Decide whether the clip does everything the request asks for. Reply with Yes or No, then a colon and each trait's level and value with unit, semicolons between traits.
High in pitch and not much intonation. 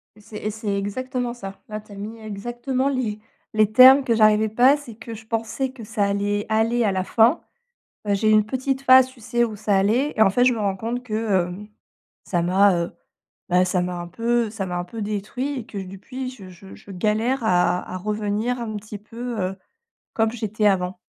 No: high, 215 Hz; average, 3.2 semitones